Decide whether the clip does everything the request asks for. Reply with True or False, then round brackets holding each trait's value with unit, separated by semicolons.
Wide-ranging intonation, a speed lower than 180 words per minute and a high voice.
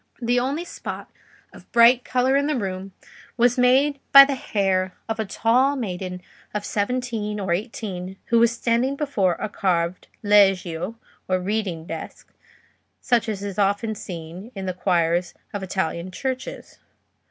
False (4.9 semitones; 150 wpm; 210 Hz)